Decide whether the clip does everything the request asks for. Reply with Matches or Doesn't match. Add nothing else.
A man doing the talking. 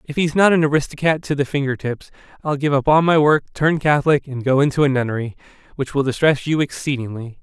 Matches